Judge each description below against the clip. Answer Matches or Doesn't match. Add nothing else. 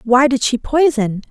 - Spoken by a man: Doesn't match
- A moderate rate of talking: Matches